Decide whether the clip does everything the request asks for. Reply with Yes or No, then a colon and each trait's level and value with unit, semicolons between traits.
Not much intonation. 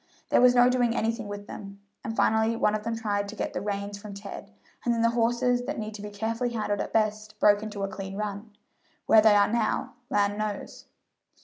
Yes: narrow, 2.1 semitones